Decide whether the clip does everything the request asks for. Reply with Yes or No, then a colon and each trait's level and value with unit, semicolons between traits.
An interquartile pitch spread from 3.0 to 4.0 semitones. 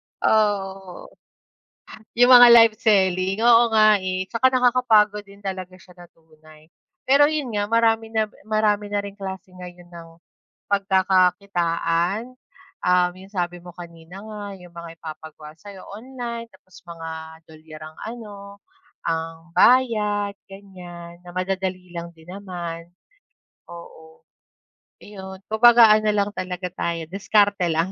Yes: average, 3.6 semitones